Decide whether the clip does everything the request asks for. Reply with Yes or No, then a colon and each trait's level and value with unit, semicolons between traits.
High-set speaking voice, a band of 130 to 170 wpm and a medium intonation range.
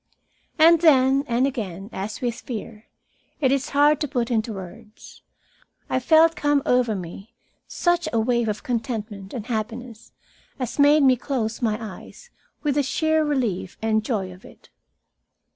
Yes: high, 240 Hz; average, 155 wpm; average, 4.7 semitones